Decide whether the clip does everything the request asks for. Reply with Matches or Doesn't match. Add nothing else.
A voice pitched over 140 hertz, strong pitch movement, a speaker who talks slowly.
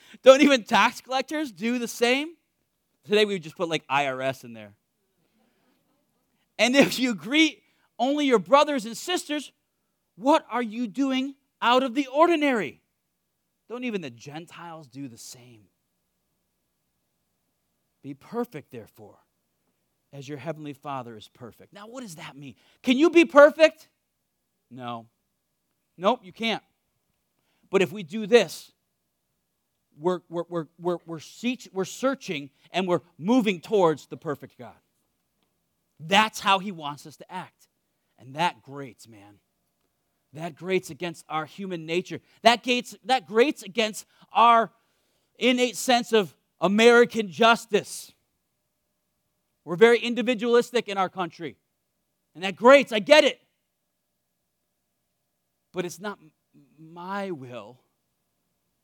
Matches